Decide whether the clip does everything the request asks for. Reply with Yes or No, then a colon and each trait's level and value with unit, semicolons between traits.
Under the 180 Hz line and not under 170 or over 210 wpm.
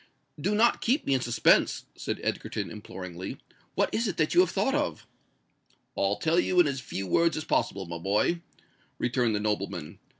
Yes: low, 135 Hz; average, 180 wpm